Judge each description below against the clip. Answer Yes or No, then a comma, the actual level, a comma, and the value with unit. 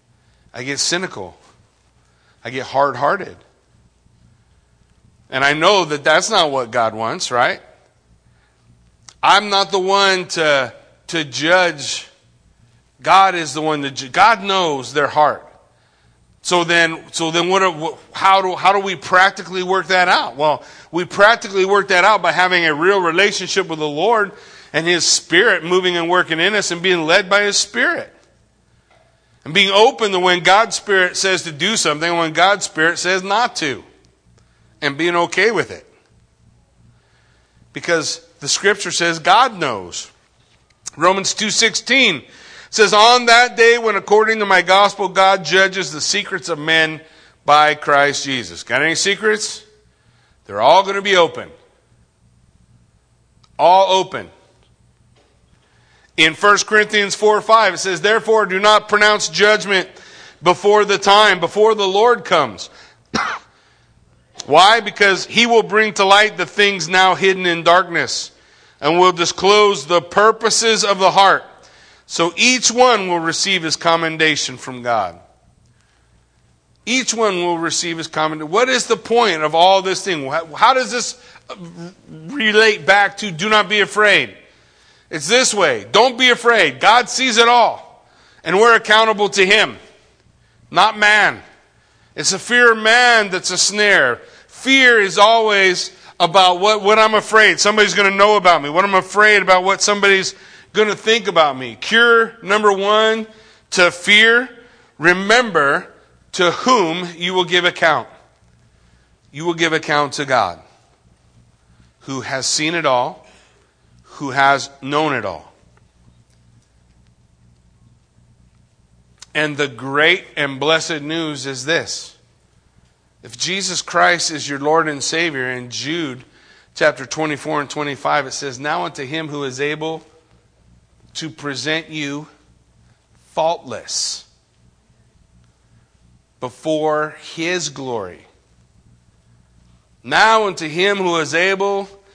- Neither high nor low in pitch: Yes, medium, 175 Hz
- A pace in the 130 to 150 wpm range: Yes, average, 140 wpm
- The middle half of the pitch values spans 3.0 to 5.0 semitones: No, wide, 5.6 semitones